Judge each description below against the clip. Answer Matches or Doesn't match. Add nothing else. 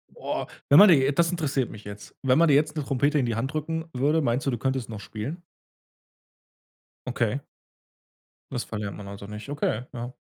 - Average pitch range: Matches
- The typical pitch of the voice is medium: Doesn't match